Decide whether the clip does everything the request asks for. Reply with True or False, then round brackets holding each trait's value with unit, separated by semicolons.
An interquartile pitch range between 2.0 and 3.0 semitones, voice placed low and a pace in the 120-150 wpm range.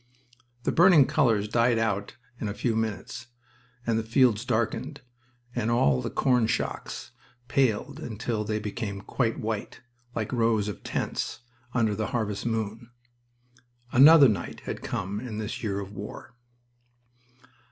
True (2.7 semitones; 115 Hz; 140 wpm)